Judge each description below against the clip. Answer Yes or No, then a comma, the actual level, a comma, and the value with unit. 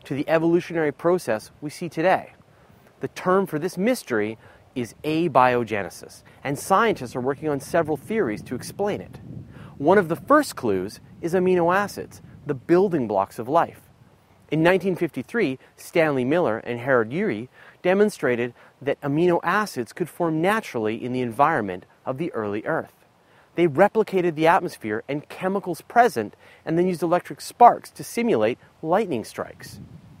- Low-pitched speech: No, medium, 155 Hz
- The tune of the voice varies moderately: No, wide, 6.3 semitones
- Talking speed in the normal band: Yes, average, 145 wpm